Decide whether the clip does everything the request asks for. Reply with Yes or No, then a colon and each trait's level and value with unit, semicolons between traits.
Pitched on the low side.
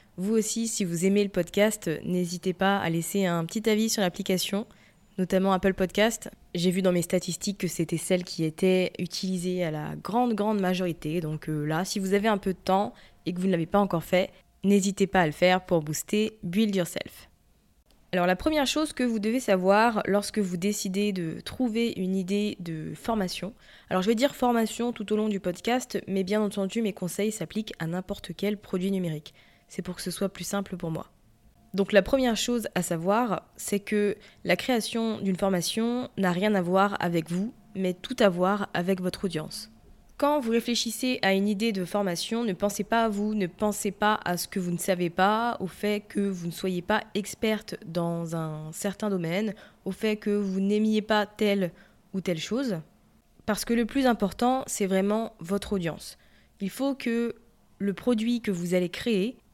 No: high, 195 Hz